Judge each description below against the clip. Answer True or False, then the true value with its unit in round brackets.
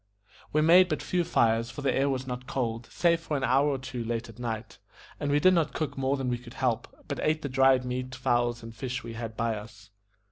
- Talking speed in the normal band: False (245 wpm)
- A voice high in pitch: False (130 Hz)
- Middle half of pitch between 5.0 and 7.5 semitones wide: False (3.2 semitones)